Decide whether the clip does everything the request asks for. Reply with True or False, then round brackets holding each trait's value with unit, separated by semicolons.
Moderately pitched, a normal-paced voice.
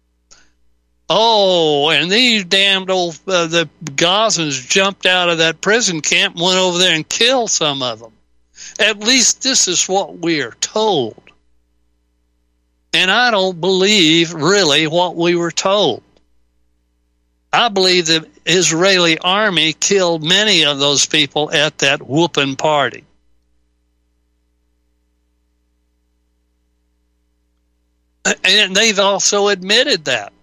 False (160 Hz; 115 wpm)